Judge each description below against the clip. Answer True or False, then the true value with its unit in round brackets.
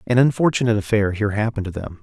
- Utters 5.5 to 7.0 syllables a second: False (7.9 syllables/s)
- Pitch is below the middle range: True (110 Hz)